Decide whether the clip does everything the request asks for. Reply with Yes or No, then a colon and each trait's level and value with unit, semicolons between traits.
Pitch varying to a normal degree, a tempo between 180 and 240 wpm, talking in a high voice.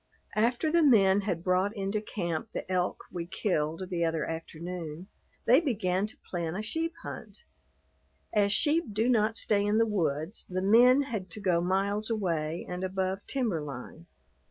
No: average, 4.1 semitones; average, 165 wpm; high, 195 Hz